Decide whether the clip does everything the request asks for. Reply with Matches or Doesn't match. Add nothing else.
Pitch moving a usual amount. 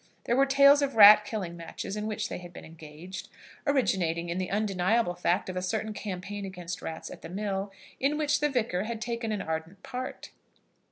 Matches